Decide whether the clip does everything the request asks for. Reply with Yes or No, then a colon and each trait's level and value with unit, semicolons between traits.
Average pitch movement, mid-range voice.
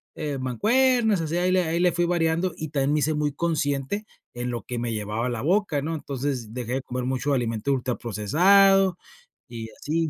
No: wide, 5.9 semitones; medium, 145 Hz